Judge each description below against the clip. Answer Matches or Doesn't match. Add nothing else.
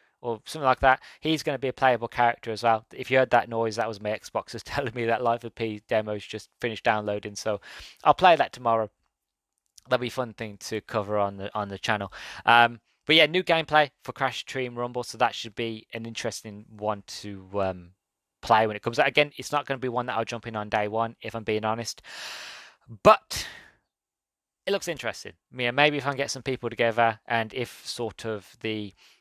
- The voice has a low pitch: Matches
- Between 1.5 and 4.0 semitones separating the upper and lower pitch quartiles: Matches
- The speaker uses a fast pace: Matches